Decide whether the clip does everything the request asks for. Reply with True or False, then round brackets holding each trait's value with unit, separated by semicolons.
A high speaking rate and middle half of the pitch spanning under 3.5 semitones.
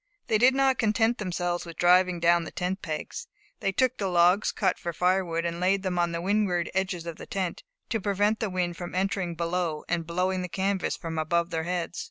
True (215 wpm; 2.4 semitones)